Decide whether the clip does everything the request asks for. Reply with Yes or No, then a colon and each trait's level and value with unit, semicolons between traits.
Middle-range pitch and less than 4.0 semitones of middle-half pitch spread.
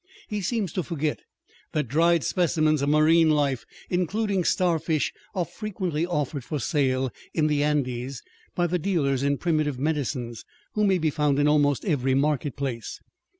Yes: medium, 150 Hz; average, 3.6 semitones